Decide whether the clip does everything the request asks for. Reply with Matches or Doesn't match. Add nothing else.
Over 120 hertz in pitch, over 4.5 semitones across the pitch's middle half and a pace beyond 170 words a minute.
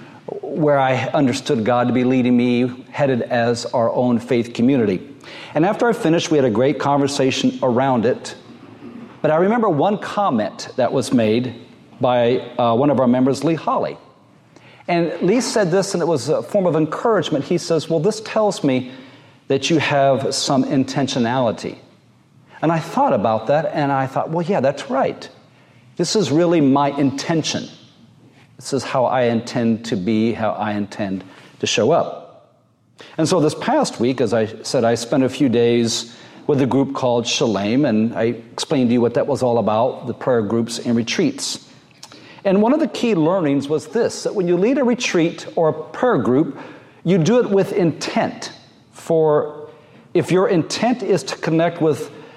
Matches